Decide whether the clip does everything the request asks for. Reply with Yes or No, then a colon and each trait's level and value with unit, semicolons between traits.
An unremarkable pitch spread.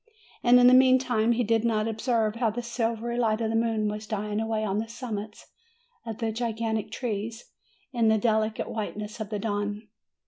No: narrow, 1.6 semitones